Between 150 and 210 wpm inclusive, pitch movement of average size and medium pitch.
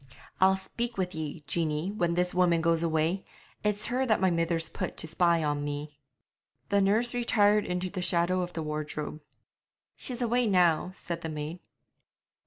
Yes: average, 170 wpm; average, 3.7 semitones; medium, 175 Hz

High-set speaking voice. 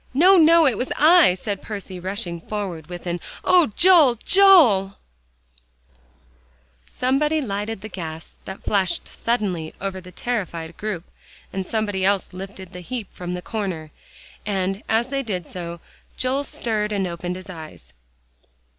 Yes: high, 200 Hz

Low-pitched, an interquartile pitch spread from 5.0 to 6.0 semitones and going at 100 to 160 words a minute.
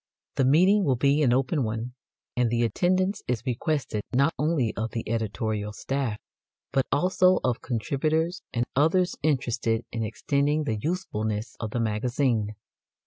Yes: low, 125 Hz; average, 5.3 semitones; average, 145 wpm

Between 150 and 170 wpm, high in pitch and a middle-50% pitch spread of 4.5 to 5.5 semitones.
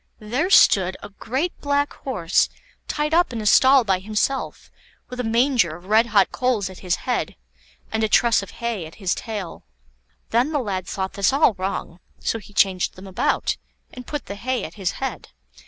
No: average, 190 wpm; high, 220 Hz; average, 5.0 semitones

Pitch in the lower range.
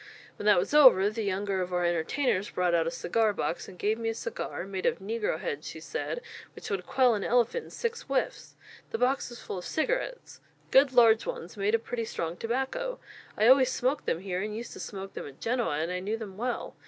No: high, 220 Hz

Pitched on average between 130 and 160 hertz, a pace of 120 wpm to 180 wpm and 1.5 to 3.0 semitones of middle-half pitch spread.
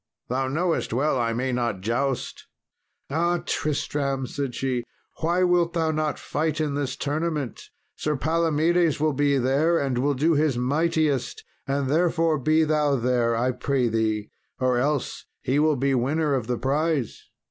No: medium, 140 Hz; average, 160 wpm; average, 3.6 semitones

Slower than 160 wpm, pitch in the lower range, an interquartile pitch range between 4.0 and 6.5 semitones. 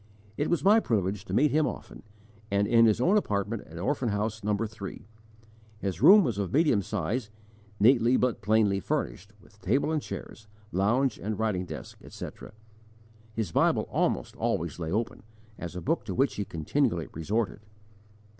No: average, 165 wpm; low, 110 Hz; average, 4.4 semitones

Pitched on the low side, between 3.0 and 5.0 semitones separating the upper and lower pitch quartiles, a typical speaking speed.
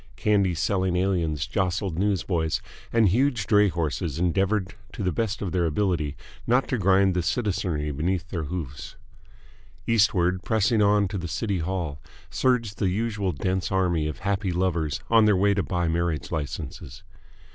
Yes: very low, 95 Hz; average, 3.3 semitones; average, 155 wpm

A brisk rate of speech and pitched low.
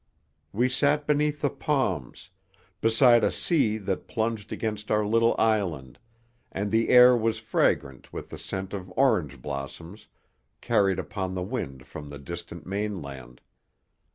No: average, 140 wpm; low, 105 Hz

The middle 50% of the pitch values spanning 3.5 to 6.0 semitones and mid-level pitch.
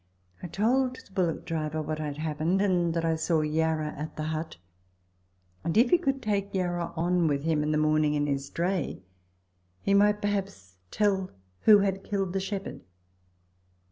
Yes: average, 4.4 semitones; medium, 170 Hz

